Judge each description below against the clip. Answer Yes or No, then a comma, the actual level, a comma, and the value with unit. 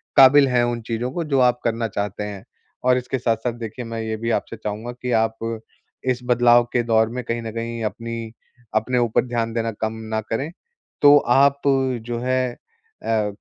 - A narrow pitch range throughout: Yes, narrow, 1.8 semitones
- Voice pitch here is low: Yes, low, 115 Hz